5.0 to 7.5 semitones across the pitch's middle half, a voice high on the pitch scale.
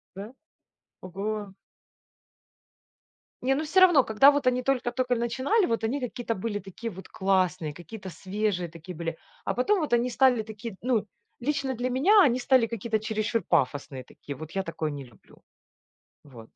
Yes: wide, 5.4 semitones; high, 220 Hz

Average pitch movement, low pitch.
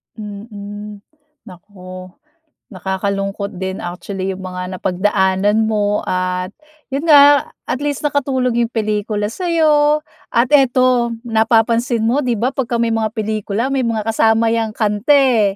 No: average, 3.7 semitones; high, 220 Hz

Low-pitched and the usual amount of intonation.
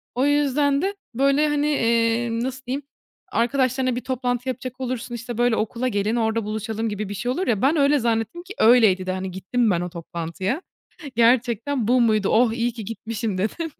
No: high, 235 Hz; average, 3.1 semitones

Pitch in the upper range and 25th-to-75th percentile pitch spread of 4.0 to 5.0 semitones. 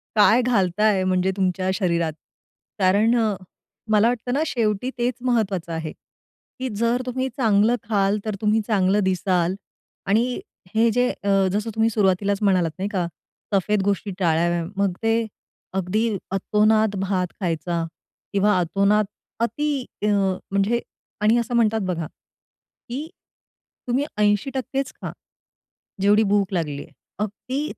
No: high, 205 Hz; average, 3.3 semitones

